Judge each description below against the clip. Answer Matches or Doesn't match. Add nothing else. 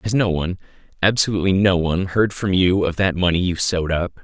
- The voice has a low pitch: Matches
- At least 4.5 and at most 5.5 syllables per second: Doesn't match